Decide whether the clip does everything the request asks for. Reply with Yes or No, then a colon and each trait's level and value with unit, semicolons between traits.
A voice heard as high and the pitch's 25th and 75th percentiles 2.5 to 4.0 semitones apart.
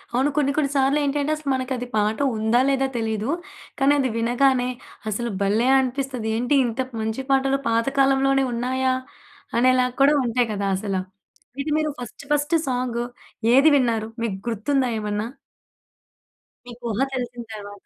Yes: very high, 250 Hz; average, 3.0 semitones